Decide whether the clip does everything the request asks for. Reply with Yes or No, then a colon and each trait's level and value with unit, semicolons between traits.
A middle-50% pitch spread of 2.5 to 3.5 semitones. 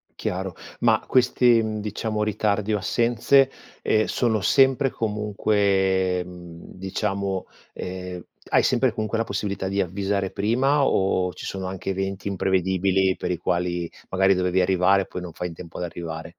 Yes: average, 2.8 semitones